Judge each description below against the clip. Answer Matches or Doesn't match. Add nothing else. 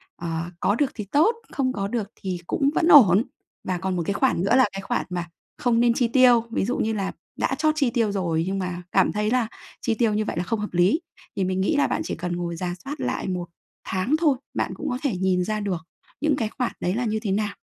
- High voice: Matches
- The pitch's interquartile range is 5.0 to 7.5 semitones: Matches